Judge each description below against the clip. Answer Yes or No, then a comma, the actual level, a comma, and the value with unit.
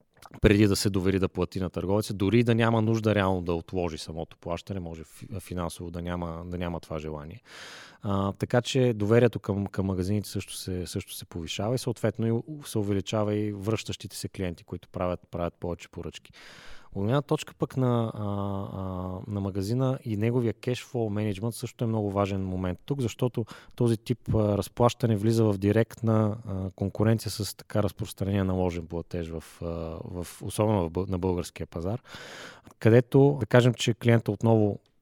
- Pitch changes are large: No, average, 4.0 semitones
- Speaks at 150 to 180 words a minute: Yes, average, 160 wpm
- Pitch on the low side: Yes, low, 105 Hz